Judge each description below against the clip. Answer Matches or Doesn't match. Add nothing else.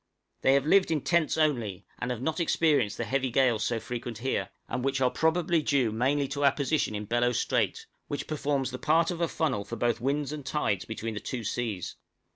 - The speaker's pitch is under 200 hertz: Matches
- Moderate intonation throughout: Matches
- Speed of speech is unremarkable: Doesn't match